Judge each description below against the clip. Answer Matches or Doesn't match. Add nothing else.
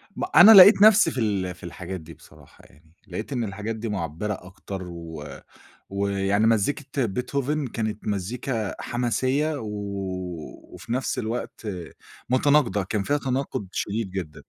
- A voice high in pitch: Doesn't match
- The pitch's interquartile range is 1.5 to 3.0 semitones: Doesn't match